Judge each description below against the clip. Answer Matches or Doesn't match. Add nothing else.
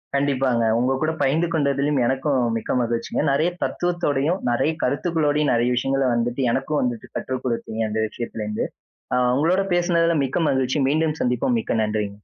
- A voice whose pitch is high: Doesn't match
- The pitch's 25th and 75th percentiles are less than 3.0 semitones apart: Doesn't match